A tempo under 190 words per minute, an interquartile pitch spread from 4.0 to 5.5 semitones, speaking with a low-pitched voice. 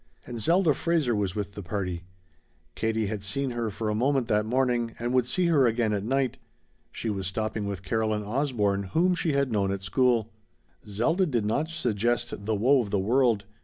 No: average, 195 wpm; average, 4.3 semitones; low, 115 Hz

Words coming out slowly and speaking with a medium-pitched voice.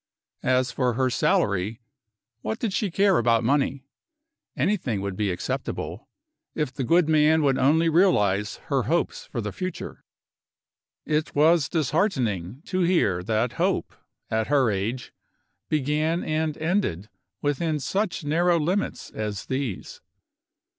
Yes: slow, 130 wpm; medium, 145 Hz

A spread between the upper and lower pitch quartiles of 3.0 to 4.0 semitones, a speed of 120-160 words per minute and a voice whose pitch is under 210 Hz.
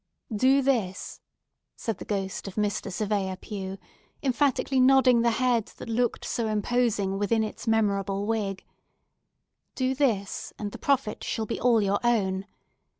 No: average, 3.6 semitones; average, 145 wpm; high, 220 Hz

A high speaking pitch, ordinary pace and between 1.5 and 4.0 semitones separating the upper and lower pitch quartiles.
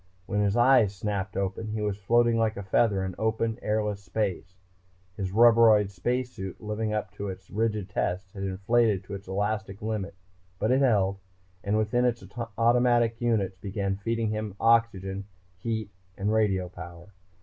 No: low, 105 Hz; average, 160 wpm; average, 2.8 semitones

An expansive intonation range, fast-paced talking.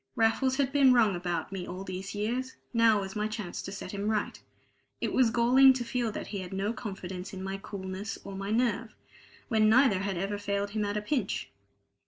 No: average, 3.3 semitones; fast, 210 wpm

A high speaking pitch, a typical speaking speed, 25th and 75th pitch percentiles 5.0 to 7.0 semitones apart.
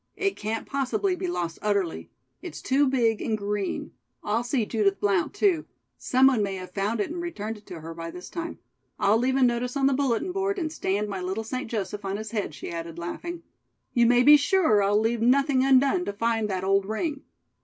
No: high, 225 Hz; fast, 215 wpm; wide, 5.6 semitones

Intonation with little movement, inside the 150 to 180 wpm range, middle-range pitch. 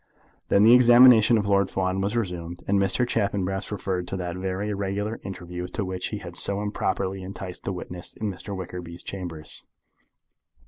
No: narrow, 2.2 semitones; average, 170 wpm; very low, 95 Hz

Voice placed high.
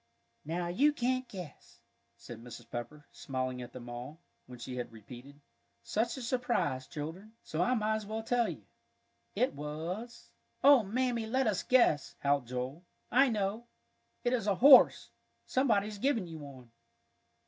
Yes: high, 195 Hz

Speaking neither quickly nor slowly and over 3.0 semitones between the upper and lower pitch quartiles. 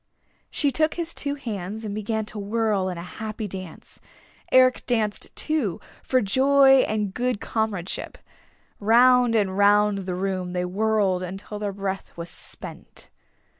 Yes: average, 145 wpm; average, 4.0 semitones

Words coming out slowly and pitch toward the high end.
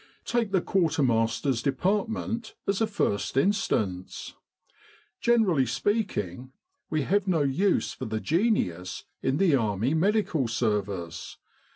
No: slow, 115 wpm; medium, 145 Hz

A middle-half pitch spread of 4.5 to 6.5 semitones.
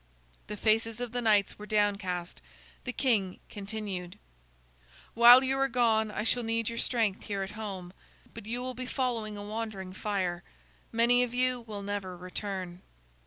No: average, 3.2 semitones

